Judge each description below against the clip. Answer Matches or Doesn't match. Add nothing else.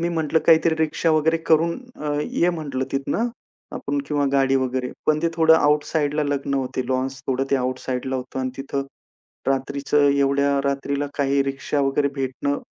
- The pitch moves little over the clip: Matches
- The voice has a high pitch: Doesn't match